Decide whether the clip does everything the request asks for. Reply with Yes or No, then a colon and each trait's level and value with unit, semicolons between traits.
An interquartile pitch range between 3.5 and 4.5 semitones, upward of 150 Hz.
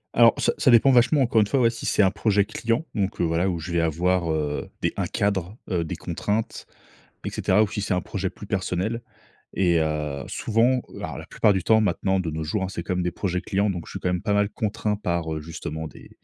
No: average, 4.1 semitones; very low, 95 Hz